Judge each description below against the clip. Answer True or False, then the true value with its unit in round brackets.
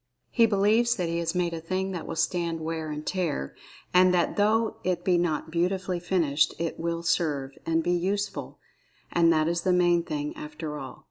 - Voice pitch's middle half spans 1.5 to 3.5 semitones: True (2.5 semitones)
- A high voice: False (175 Hz)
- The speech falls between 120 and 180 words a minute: False (200 wpm)